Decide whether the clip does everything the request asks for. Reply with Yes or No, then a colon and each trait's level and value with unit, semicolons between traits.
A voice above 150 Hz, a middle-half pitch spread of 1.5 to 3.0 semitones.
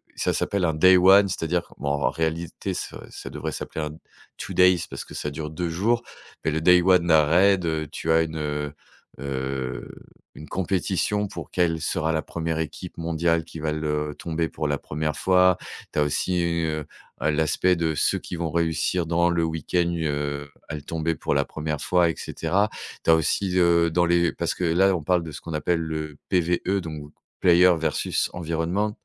No: very low, 80 Hz; narrow, 2.4 semitones